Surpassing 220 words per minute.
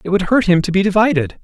Yes: fast, 295 wpm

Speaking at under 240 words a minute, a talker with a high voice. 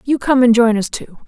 No: fast, 280 wpm; high, 240 Hz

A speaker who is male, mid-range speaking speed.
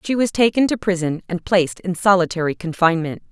No: female; average, 180 wpm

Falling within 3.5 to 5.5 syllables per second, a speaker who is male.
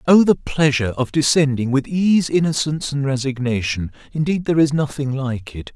Yes: 5.4 syllables/s; male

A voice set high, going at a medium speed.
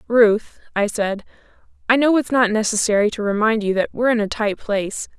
Yes: high, 220 Hz; average, 195 wpm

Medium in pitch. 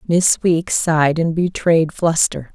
Yes: medium, 165 Hz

